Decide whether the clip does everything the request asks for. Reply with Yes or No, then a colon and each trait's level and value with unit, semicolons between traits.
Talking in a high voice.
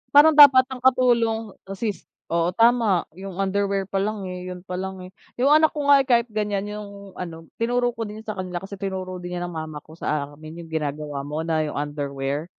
Yes: high, 195 Hz